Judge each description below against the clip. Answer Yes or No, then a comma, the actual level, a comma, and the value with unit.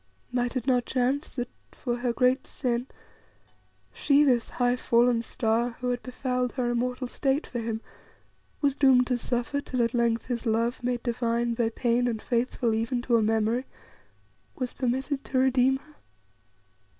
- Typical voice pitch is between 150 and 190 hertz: No, high, 245 Hz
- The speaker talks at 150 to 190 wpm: Yes, average, 160 wpm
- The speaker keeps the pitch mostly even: Yes, narrow, 1.5 semitones